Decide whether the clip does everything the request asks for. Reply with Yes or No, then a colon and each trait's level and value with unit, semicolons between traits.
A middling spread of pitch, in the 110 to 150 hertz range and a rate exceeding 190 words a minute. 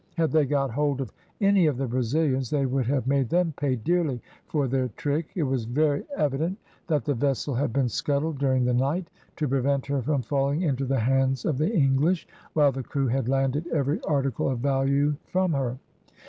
No: narrow, 2.3 semitones; medium, 140 Hz; average, 200 wpm